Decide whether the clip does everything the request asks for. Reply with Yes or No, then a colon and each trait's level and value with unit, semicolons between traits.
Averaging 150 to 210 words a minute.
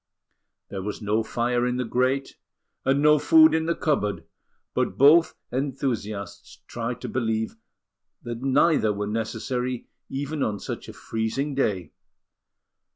No: slow, 135 wpm